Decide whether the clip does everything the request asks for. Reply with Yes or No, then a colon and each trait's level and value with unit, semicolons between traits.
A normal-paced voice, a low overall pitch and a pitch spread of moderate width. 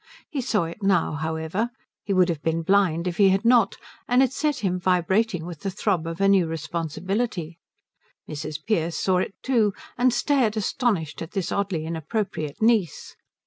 No: average, 175 wpm; medium, 185 Hz; average, 4.7 semitones